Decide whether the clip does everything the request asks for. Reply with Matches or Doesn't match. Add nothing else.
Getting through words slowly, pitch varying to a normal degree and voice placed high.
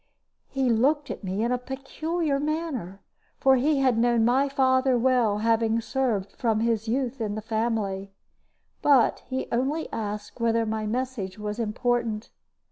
Doesn't match